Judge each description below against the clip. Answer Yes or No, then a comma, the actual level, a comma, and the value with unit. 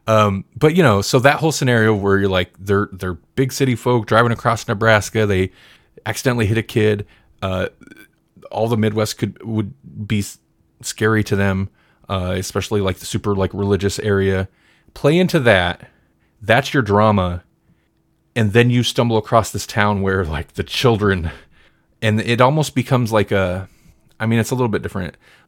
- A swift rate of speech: No, average, 170 wpm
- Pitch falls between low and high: No, low, 105 Hz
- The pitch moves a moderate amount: Yes, average, 3.4 semitones